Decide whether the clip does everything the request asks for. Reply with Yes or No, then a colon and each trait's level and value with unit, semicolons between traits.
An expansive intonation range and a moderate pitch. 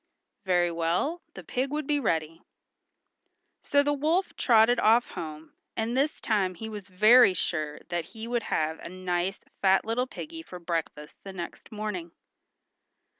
No: wide, 6.1 semitones; high, 200 Hz